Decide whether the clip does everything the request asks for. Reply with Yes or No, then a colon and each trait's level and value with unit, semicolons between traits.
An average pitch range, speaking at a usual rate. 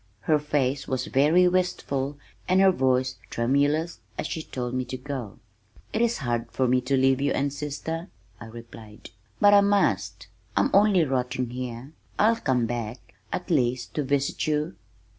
Yes: average, 4.2 semitones; average, 165 wpm